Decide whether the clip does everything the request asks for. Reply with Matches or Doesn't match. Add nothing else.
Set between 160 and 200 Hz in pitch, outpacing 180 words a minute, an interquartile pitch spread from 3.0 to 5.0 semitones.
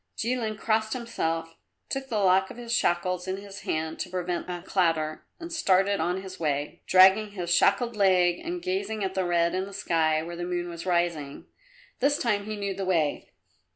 Matches